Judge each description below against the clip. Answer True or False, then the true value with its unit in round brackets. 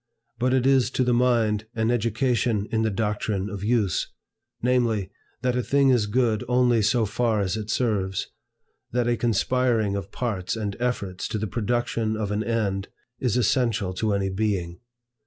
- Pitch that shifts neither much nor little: True (3.1 semitones)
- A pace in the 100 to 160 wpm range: False (170 wpm)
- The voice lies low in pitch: True (110 Hz)